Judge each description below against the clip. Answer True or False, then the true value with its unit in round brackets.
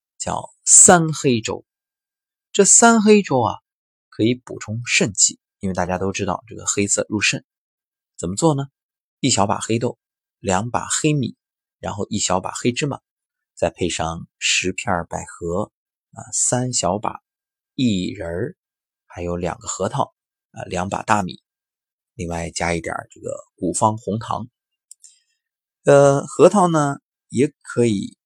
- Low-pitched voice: True (110 Hz)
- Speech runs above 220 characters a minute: False (195 characters per minute)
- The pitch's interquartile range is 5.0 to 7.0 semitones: False (7.8 semitones)